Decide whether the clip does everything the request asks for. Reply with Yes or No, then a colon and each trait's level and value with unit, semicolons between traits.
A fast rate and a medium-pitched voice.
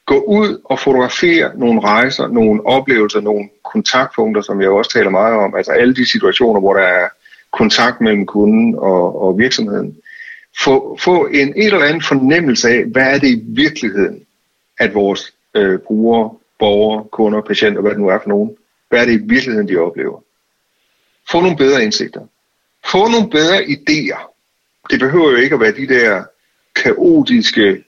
No: average, 170 wpm; medium, 175 Hz